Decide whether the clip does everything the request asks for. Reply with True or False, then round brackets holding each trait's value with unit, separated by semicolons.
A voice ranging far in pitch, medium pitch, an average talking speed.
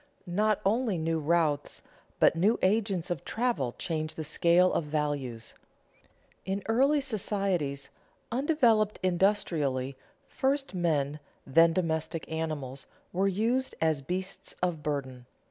False (5.8 semitones; 170 Hz; 120 wpm)